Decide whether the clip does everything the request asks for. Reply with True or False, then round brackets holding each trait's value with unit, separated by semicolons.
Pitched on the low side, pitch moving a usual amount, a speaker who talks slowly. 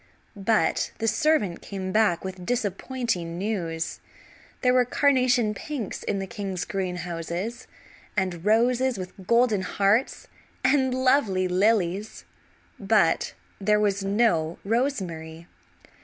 False (200 Hz; 4.6 semitones; 110 wpm)